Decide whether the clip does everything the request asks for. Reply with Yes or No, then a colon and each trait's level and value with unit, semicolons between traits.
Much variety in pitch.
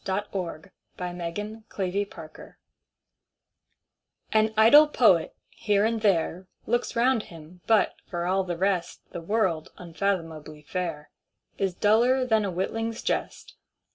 No: average, 4.2 semitones